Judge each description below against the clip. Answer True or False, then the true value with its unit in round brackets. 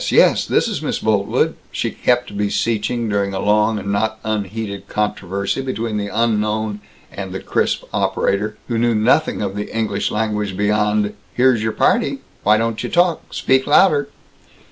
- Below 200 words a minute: True (160 wpm)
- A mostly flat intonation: True (2.0 semitones)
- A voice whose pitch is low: True (105 Hz)